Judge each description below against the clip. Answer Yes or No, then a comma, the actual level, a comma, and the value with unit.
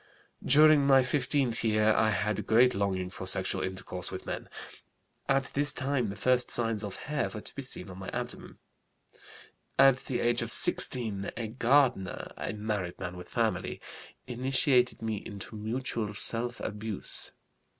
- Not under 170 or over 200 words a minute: No, average, 155 wpm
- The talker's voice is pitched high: No, low, 115 Hz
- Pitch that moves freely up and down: No, average, 4.3 semitones